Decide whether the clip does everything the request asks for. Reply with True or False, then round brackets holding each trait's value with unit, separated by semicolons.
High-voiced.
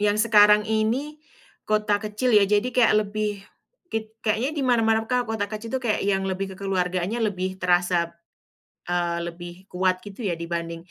True (205 Hz)